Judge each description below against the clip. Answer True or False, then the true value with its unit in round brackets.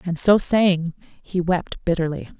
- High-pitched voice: False (175 Hz)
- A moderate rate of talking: True (150 wpm)